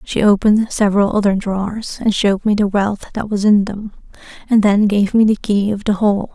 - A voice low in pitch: No, high, 205 Hz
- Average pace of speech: No, fast, 215 wpm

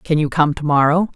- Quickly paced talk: Yes, fast, 260 wpm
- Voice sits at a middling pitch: Yes, medium, 155 Hz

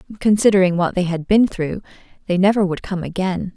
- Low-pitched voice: No, medium, 185 Hz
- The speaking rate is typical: Yes, average, 185 wpm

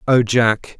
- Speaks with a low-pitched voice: Yes, low, 115 Hz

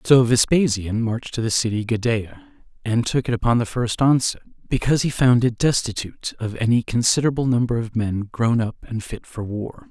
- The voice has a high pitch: No, low, 120 Hz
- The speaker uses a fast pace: No, average, 190 wpm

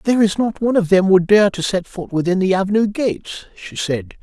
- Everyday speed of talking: No, fast, 240 wpm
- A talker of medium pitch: No, high, 195 Hz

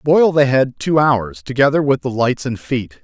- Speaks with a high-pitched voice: No, low, 130 Hz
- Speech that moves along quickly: Yes, fast, 215 wpm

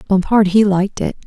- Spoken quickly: No, average, 190 wpm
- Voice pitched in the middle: No, high, 195 Hz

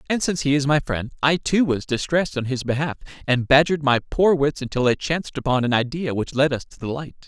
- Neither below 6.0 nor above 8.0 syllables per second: Yes, 6.1 syllables/s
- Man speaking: Yes, male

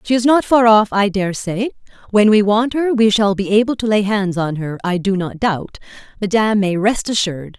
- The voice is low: No, high, 205 Hz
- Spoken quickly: Yes, fast, 230 wpm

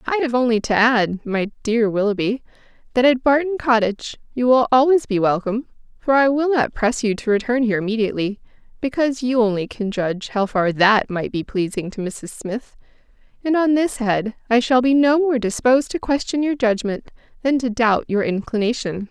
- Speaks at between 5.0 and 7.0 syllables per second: Yes, 5.4 syllables/s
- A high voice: Yes, high, 235 Hz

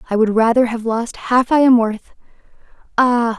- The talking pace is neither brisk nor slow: Yes, average, 175 wpm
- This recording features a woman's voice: Yes, female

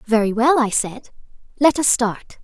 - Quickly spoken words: No, average, 170 wpm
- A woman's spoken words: Yes, female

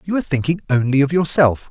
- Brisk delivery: Yes, fast, 210 wpm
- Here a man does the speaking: Yes, male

